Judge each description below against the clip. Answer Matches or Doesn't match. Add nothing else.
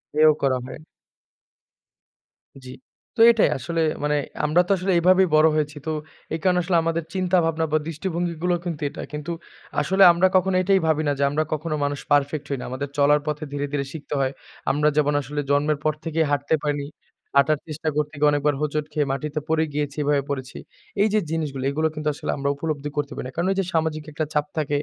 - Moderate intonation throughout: Doesn't match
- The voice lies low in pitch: Doesn't match